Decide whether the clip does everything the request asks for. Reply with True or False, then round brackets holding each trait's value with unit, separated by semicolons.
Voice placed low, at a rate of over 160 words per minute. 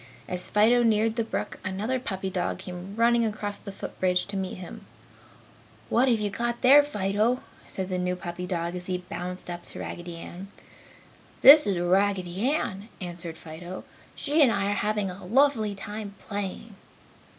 False (195 Hz; 170 wpm)